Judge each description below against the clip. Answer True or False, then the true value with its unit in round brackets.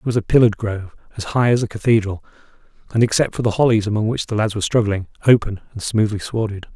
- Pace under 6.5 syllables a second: False (7.0 syllables/s)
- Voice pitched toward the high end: False (110 Hz)